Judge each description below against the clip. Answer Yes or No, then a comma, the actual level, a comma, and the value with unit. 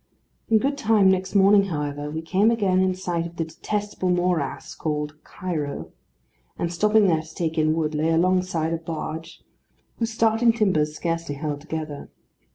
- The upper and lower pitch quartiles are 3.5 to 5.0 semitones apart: Yes, average, 4.0 semitones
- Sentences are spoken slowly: No, average, 165 wpm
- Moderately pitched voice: Yes, medium, 170 Hz